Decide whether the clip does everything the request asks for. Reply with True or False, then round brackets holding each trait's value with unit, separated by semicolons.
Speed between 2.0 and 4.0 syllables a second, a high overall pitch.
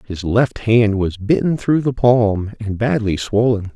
False (3.9 syllables/s; 110 Hz)